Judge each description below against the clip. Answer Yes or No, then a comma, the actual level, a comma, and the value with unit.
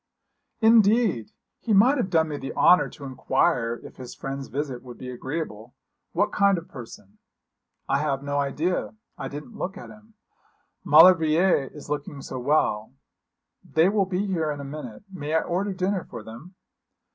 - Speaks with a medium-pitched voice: Yes, medium, 155 Hz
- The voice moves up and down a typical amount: No, wide, 5.7 semitones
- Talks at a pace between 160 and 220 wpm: Yes, average, 170 wpm